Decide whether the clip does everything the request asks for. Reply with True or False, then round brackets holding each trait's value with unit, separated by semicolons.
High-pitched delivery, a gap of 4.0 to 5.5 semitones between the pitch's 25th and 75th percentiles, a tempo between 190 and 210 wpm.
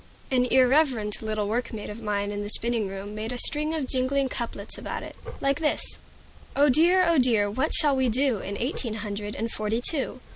True (240 Hz; 4.6 semitones; 195 wpm)